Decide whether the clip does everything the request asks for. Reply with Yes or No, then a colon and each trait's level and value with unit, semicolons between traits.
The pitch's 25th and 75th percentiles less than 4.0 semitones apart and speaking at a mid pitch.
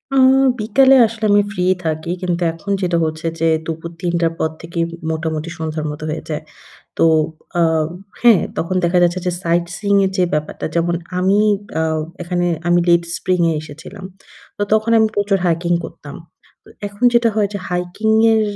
Yes: average, 3.6 semitones; medium, 175 Hz